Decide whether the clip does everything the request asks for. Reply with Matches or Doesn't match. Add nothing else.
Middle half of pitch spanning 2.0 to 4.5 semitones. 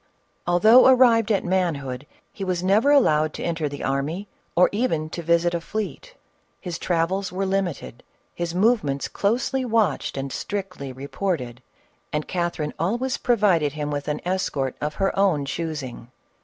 Doesn't match